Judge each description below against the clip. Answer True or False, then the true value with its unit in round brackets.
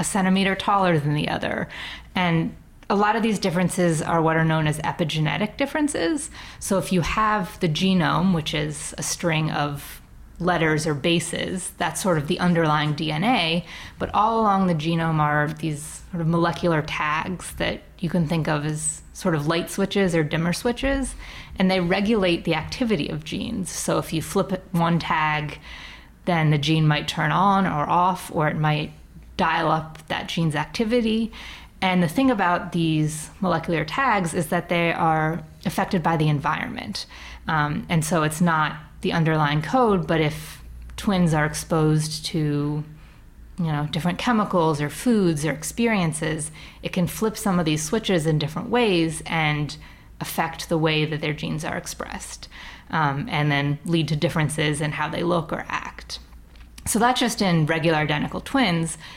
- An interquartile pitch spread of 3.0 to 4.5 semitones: True (3.4 semitones)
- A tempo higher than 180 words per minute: False (170 wpm)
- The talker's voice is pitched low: False (165 Hz)